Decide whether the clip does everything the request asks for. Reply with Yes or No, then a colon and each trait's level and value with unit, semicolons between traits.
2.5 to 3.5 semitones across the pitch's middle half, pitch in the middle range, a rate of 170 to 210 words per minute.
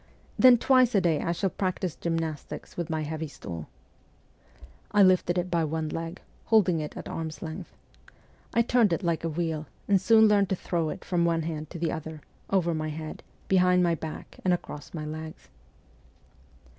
Yes: average, 2.8 semitones; medium, 170 Hz; average, 180 wpm